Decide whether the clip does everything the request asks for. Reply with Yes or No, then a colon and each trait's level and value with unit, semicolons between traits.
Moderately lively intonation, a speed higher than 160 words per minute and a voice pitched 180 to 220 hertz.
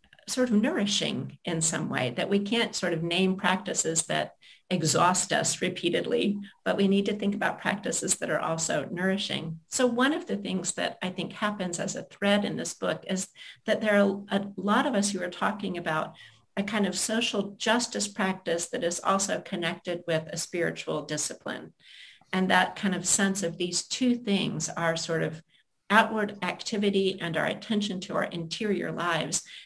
Yes: average, 3.2 semitones; average, 180 wpm; high, 190 Hz